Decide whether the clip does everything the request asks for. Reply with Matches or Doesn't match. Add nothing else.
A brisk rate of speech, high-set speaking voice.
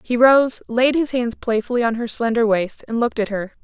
Matches